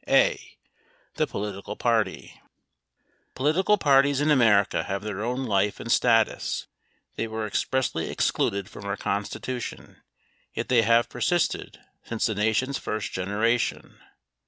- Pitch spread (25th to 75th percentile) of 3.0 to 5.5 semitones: Yes, average, 4.1 semitones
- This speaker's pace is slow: Yes, slow, 130 wpm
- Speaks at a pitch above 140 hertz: No, low, 115 Hz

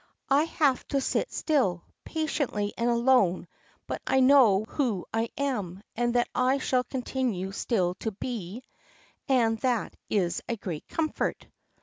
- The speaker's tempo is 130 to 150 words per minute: Yes, average, 140 wpm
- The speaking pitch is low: No, high, 240 Hz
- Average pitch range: Yes, average, 4.7 semitones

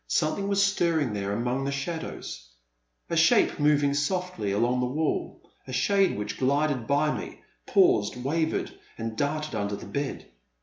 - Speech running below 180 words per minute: Yes, average, 165 wpm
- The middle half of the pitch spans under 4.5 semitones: No, wide, 5.6 semitones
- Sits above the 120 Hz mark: Yes, medium, 140 Hz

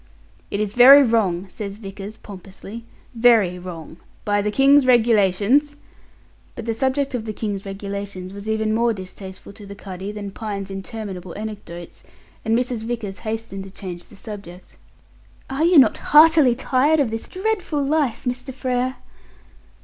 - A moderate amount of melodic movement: Yes, average, 4.2 semitones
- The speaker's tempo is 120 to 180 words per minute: Yes, average, 155 wpm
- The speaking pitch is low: No, high, 215 Hz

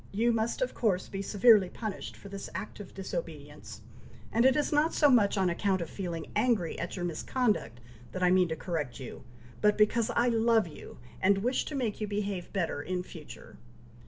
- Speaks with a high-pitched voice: Yes, high, 200 Hz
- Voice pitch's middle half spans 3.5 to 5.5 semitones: Yes, average, 4.4 semitones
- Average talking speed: Yes, average, 195 wpm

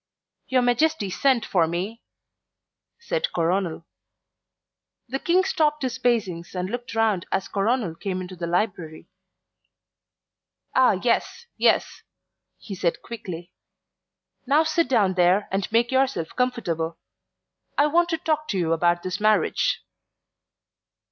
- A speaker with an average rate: No, slow, 125 wpm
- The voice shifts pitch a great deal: Yes, wide, 6.6 semitones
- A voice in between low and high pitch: No, high, 215 Hz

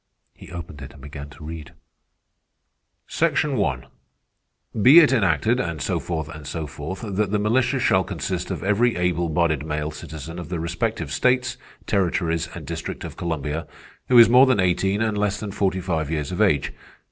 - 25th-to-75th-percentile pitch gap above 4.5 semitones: Yes, wide, 5.4 semitones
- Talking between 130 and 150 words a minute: No, average, 180 wpm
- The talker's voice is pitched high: No, very low, 85 Hz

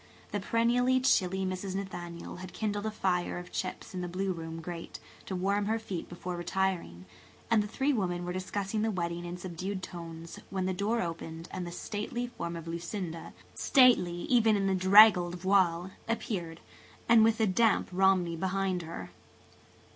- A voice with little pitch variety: No, average, 3.0 semitones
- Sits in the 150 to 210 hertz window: Yes, medium, 185 Hz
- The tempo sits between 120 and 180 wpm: Yes, average, 170 wpm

